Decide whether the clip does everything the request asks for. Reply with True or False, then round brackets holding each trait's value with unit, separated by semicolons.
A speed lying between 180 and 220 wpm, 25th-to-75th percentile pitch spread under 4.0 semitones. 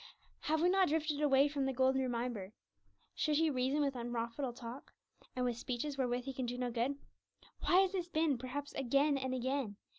True (190 wpm; 3.1 semitones)